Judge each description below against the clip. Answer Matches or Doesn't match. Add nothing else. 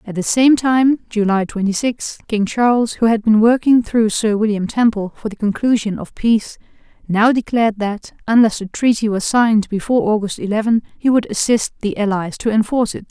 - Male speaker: Doesn't match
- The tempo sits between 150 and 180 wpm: Doesn't match